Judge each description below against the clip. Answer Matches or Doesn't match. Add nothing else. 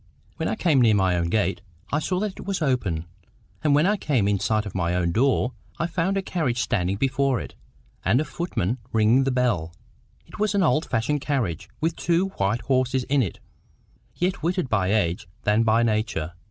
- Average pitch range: Doesn't match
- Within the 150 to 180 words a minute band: Doesn't match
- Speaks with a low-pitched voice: Matches